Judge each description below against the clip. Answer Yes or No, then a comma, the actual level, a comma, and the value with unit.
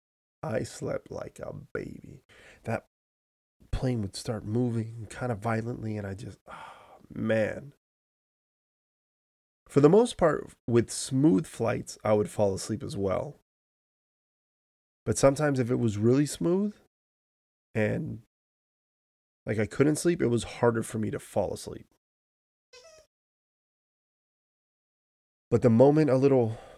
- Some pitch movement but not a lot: Yes, average, 4.4 semitones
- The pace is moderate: No, slow, 125 wpm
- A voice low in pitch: Yes, low, 115 Hz